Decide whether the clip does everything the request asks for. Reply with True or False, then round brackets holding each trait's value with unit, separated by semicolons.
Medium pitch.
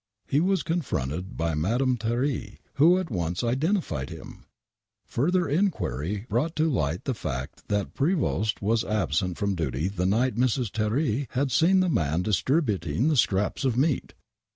False (115 Hz)